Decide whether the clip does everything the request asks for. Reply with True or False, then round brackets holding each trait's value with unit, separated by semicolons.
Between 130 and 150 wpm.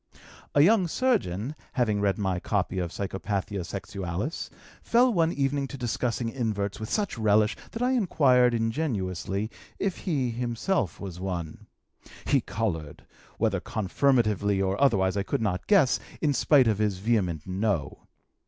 True (145 wpm)